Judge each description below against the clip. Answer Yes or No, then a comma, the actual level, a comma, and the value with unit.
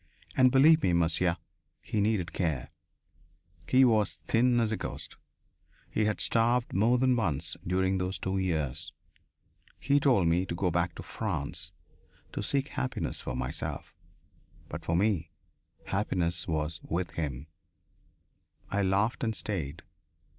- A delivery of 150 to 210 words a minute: No, average, 140 wpm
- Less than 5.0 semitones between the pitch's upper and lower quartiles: No, average, 5.3 semitones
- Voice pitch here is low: Yes, very low, 95 Hz